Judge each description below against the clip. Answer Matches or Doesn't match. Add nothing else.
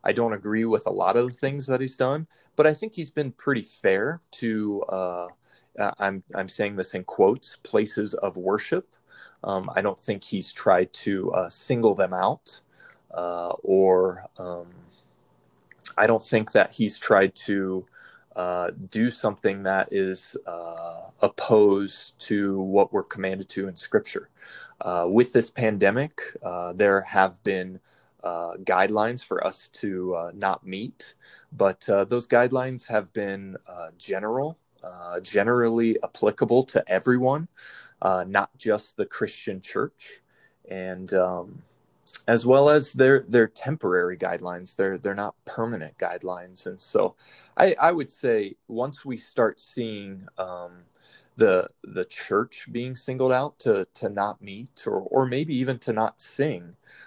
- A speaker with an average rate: Matches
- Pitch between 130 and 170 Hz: Doesn't match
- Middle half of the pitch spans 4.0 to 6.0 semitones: Matches